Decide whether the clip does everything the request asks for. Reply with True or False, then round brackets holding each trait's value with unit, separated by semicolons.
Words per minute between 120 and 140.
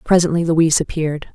True (135 wpm)